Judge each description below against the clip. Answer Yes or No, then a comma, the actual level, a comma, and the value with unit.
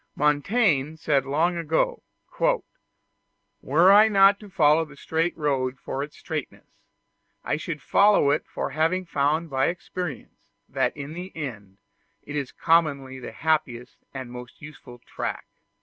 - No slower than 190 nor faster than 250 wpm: No, average, 140 wpm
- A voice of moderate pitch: Yes, medium, 150 Hz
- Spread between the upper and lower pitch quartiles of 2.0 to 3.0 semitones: No, average, 3.7 semitones